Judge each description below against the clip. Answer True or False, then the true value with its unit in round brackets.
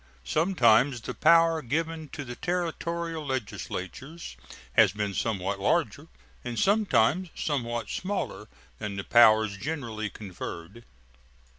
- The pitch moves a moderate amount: False (7.2 semitones)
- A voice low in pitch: True (125 Hz)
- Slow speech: True (110 wpm)